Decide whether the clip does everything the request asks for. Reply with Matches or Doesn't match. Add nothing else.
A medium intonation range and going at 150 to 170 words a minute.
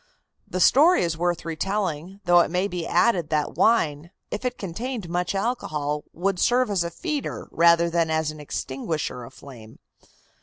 Matches